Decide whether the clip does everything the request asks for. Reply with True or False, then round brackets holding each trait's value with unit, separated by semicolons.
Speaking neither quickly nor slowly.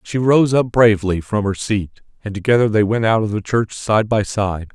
False (240 wpm)